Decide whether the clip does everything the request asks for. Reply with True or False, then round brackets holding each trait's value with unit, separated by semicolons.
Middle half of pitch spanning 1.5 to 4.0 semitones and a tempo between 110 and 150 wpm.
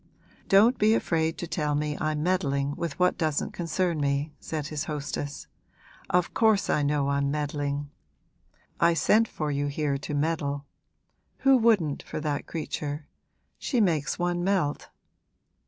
True (3.4 semitones; 145 wpm)